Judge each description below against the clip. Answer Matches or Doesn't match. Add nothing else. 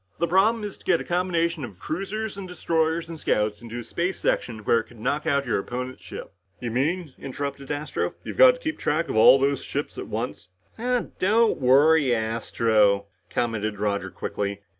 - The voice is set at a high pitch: Doesn't match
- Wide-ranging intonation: Matches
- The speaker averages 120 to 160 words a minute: Doesn't match